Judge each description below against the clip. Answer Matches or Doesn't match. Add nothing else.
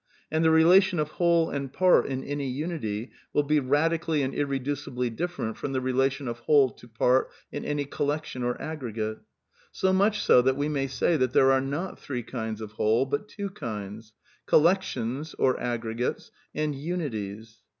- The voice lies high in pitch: Doesn't match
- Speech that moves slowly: Doesn't match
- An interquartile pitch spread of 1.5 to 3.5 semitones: Doesn't match